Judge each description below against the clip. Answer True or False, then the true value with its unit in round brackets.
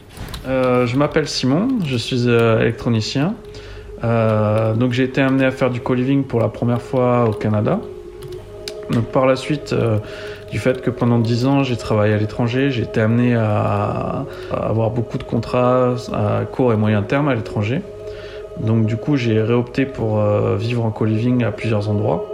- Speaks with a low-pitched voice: True (120 Hz)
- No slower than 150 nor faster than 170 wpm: False (180 wpm)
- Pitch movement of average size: True (3.4 semitones)